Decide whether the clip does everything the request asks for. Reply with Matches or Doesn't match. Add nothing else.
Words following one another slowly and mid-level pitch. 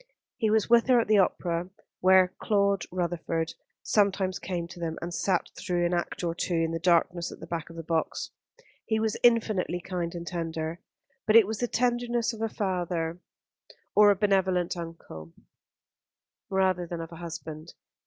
Doesn't match